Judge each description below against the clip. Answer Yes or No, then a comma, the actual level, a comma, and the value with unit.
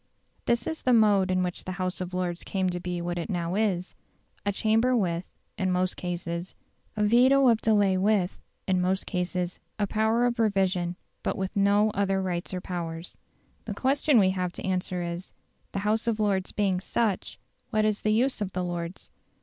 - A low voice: No, high, 190 Hz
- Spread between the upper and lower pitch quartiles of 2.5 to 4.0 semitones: Yes, average, 3.1 semitones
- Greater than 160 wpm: Yes, average, 190 wpm